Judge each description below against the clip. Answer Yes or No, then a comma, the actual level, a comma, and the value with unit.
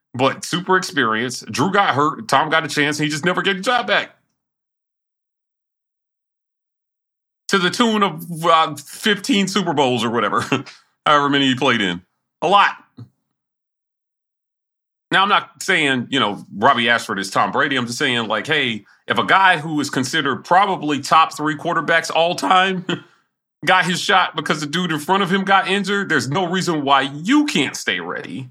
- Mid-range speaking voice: Yes, medium, 160 Hz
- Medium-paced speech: Yes, average, 175 wpm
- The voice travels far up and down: No, average, 5.0 semitones